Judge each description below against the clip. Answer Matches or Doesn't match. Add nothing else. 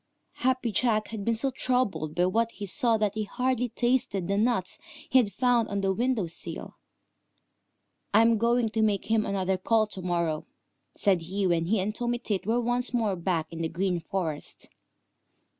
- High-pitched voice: Matches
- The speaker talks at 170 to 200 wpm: Matches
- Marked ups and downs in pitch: Doesn't match